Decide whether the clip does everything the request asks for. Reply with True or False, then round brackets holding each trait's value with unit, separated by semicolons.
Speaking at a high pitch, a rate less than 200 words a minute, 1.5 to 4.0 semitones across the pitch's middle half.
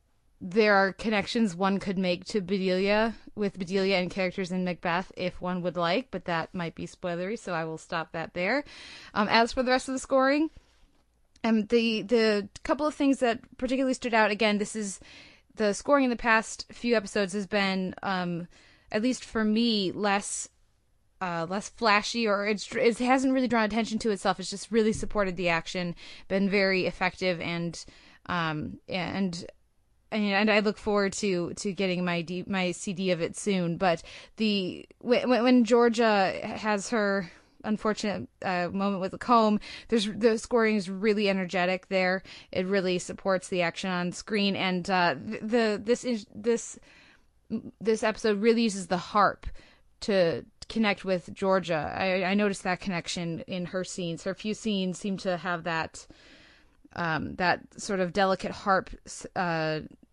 True (200 Hz; 170 wpm; 3.4 semitones)